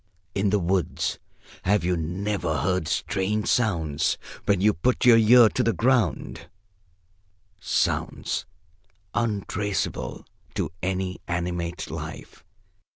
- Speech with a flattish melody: No, average, 3.4 semitones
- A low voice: Yes, very low, 95 Hz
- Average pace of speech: No, slow, 105 wpm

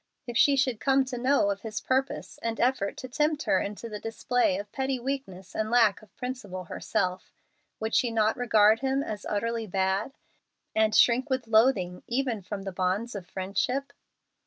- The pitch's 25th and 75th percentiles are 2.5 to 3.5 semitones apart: No, average, 4.4 semitones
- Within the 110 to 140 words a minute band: No, average, 180 wpm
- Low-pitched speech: No, high, 225 Hz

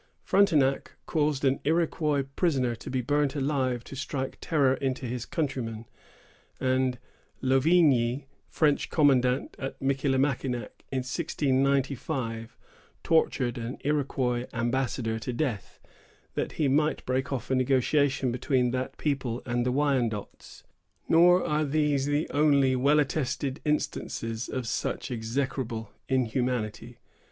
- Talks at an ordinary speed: No, slow, 120 wpm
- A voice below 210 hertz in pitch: Yes, low, 135 Hz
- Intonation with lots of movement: No, average, 2.7 semitones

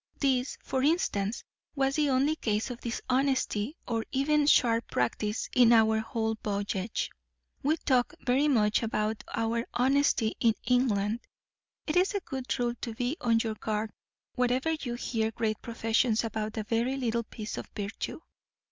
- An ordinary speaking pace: Yes, average, 155 wpm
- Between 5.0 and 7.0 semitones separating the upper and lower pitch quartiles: No, average, 3.3 semitones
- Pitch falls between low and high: No, high, 235 Hz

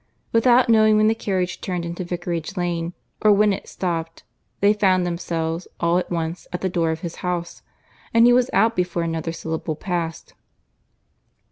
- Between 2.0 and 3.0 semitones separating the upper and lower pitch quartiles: No, average, 3.4 semitones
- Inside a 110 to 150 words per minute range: No, average, 170 wpm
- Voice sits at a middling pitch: Yes, medium, 180 Hz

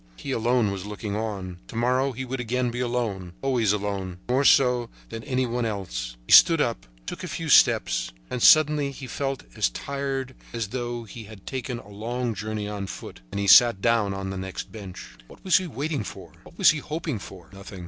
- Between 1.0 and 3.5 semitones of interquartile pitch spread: No, average, 4.5 semitones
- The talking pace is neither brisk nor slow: No, fast, 210 wpm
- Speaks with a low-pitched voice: Yes, low, 115 Hz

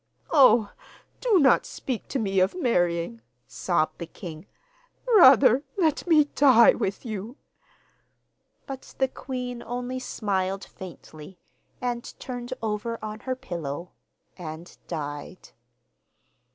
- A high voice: Yes, high, 230 Hz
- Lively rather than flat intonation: Yes, wide, 5.9 semitones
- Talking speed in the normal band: No, slow, 110 wpm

